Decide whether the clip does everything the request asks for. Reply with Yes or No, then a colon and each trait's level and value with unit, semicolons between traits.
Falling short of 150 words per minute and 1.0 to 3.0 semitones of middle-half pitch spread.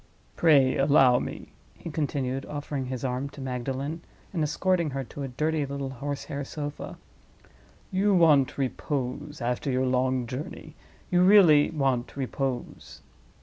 Yes: slow, 135 wpm; average, 2.7 semitones